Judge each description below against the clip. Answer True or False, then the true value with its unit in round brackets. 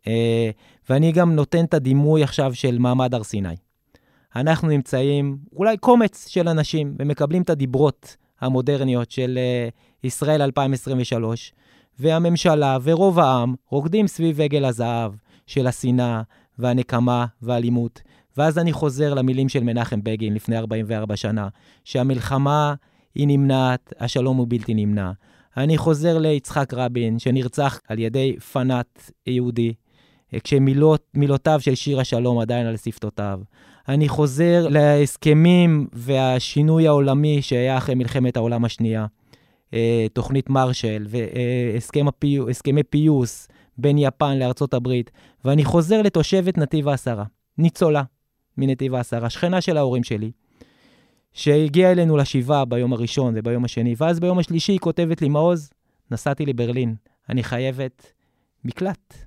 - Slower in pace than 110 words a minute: False (120 wpm)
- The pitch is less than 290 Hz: True (135 Hz)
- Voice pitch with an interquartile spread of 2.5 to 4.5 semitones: True (3.8 semitones)